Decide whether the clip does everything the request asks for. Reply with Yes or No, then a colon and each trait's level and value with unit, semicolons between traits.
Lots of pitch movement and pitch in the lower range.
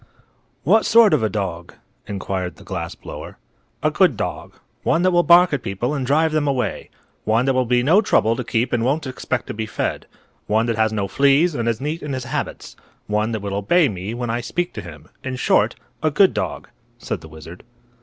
Yes: wide, 5.9 semitones; low, 120 Hz